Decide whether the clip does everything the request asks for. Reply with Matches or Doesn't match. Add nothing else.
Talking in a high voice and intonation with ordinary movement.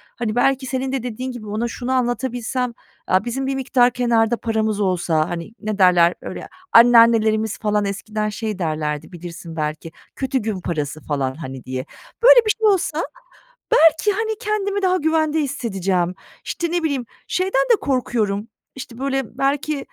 Doesn't match